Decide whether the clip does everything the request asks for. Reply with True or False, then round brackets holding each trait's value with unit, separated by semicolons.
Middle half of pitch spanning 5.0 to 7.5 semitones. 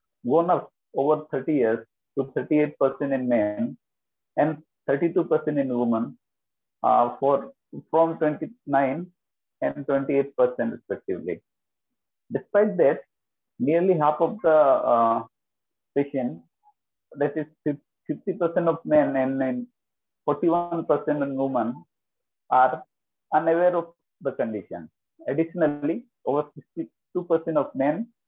False (3.7 semitones)